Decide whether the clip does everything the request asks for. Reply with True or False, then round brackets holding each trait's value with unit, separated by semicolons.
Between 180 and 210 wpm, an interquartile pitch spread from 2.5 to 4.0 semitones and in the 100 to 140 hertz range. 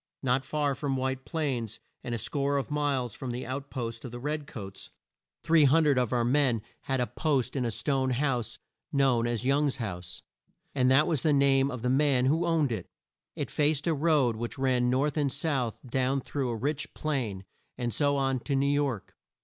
True (200 wpm; 2.8 semitones; 135 Hz)